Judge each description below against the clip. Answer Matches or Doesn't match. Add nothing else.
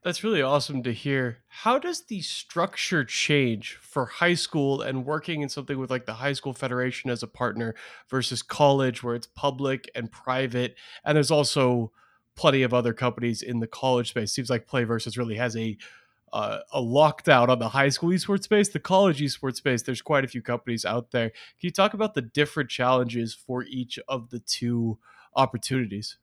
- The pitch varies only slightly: Doesn't match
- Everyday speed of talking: Matches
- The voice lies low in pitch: Matches